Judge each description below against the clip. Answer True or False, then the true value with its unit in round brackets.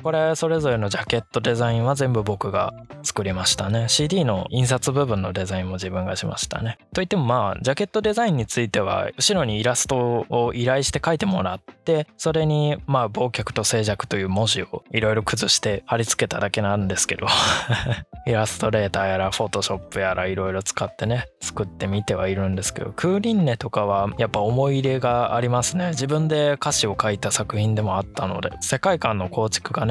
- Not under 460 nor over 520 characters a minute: False (425 characters per minute)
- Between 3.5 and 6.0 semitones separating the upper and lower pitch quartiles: True (5.3 semitones)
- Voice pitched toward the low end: True (115 Hz)